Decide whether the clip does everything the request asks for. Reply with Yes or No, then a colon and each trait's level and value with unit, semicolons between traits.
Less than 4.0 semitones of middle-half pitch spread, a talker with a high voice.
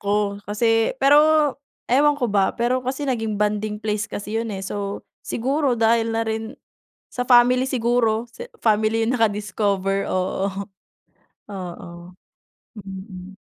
Yes: average, 3.3 semitones; high, 225 Hz